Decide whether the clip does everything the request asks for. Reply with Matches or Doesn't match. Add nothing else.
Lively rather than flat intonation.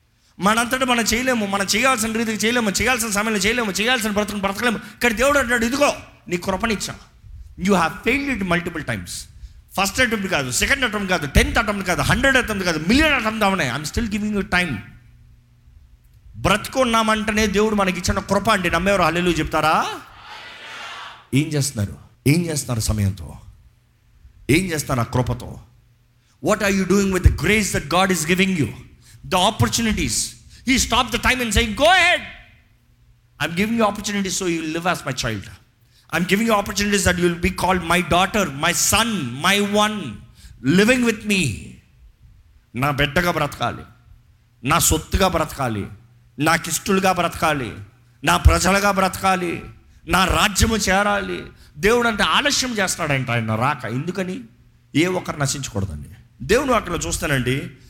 Matches